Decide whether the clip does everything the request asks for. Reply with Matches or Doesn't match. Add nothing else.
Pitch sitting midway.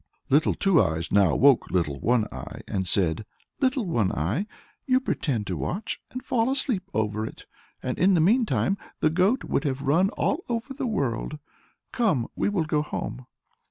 Matches